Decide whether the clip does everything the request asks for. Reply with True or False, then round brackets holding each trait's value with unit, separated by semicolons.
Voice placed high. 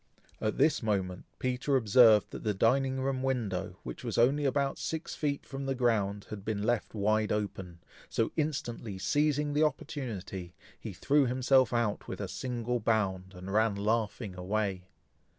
False (115 Hz)